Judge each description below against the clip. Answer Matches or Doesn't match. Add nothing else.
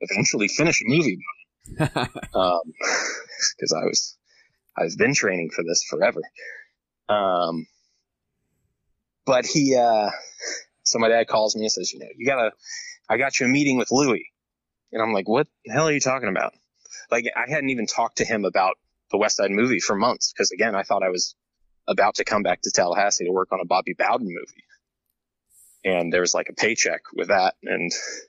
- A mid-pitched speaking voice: Doesn't match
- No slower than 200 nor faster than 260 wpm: Doesn't match